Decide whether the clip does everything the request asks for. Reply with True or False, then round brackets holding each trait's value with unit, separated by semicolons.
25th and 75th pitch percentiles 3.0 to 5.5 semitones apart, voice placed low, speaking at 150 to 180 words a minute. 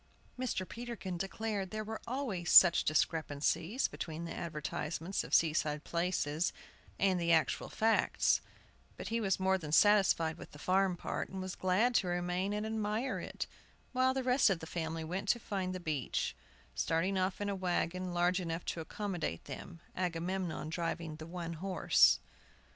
False (3.5 semitones; 180 Hz; 165 wpm)